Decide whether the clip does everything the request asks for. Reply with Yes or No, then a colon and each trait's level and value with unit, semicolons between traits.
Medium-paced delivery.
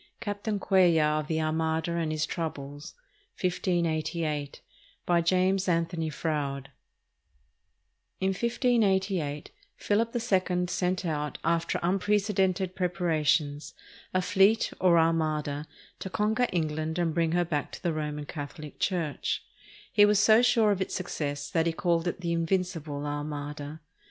No: slow, 130 wpm